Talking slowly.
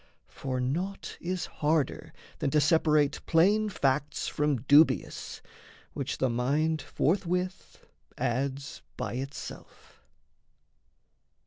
Yes: slow, 95 wpm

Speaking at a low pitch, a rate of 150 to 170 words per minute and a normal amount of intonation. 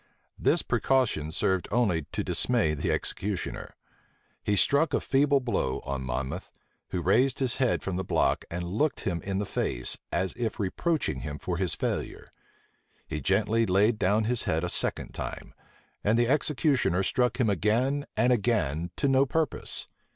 No: low, 105 Hz; average, 165 wpm; wide, 6.4 semitones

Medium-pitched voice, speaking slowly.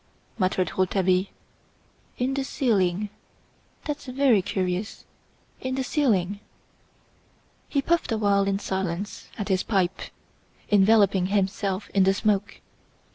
No: high, 200 Hz; slow, 110 wpm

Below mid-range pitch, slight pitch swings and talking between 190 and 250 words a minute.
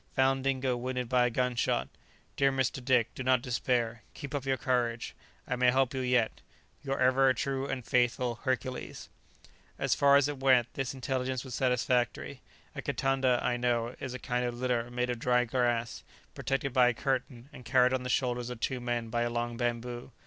Yes: low, 125 Hz; narrow, 1.5 semitones; average, 195 wpm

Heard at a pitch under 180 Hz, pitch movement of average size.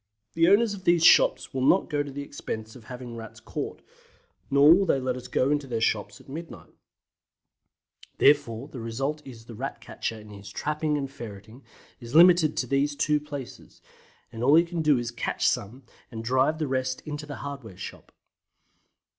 Yes: low, 135 Hz; average, 4.3 semitones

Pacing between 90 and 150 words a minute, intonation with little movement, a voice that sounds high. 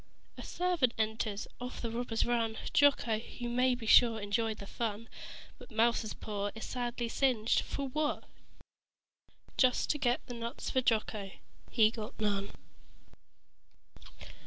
Yes: slow, 135 wpm; narrow, 2.3 semitones; high, 230 Hz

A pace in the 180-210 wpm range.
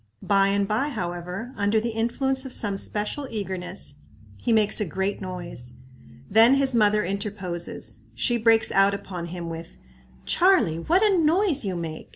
No: average, 160 wpm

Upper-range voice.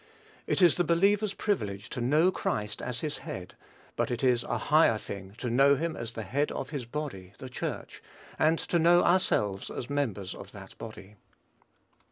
No: low, 125 Hz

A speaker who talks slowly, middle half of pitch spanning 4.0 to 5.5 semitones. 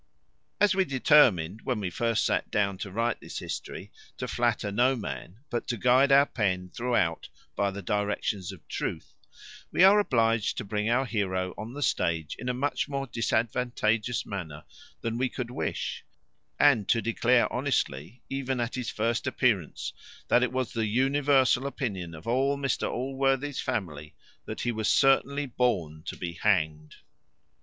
No: average, 165 wpm; average, 4.8 semitones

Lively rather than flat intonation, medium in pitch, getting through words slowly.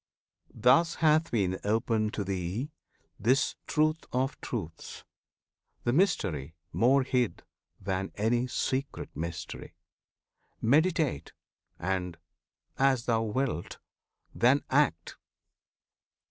No: wide, 6.2 semitones; low, 120 Hz; slow, 90 wpm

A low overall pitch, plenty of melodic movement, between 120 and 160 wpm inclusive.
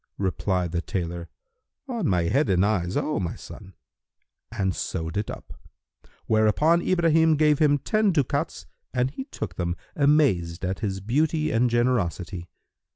Yes: low, 110 Hz; wide, 8.8 semitones; average, 145 wpm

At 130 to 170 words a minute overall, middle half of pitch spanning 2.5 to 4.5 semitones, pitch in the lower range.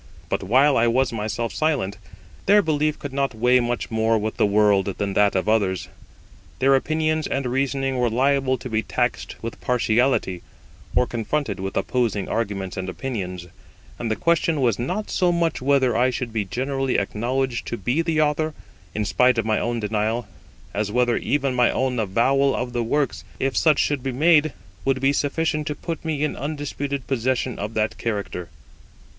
No: average, 180 wpm; average, 4.2 semitones; low, 125 Hz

